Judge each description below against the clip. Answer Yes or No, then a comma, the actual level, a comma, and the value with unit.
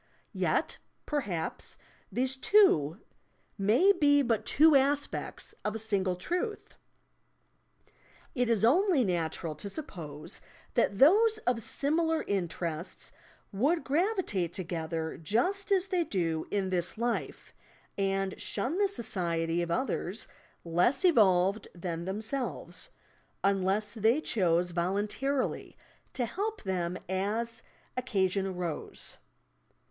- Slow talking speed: Yes, slow, 110 wpm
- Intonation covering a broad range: Yes, wide, 7.7 semitones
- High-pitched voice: Yes, high, 210 Hz